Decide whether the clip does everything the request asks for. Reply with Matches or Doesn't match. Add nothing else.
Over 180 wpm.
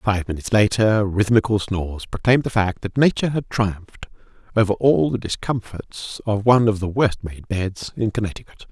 Doesn't match